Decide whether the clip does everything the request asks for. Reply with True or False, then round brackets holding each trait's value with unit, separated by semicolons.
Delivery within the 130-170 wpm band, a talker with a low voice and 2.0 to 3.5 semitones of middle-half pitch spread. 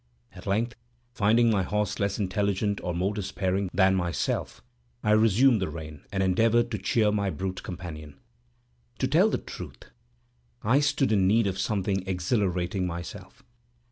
True (150 wpm; 100 Hz; 2.7 semitones)